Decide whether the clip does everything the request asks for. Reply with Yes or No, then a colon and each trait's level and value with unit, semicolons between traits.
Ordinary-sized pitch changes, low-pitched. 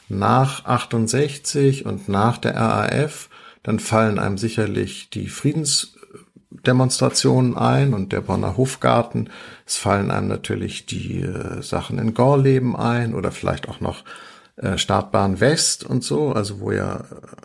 Yes: average, 4.2 semitones; low, 120 Hz